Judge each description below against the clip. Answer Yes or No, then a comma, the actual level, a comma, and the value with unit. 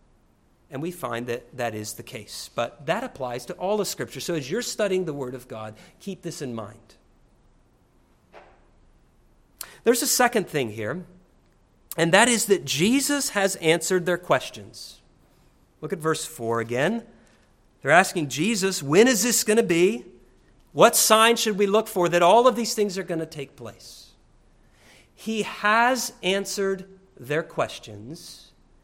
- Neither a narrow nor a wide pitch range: No, wide, 8.1 semitones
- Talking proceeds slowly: No, average, 160 wpm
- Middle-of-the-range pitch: Yes, medium, 180 Hz